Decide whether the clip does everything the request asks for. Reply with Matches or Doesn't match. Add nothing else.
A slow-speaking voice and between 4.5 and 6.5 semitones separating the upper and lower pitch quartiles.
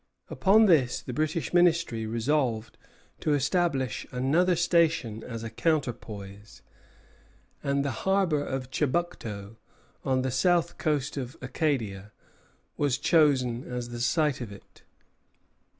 Matches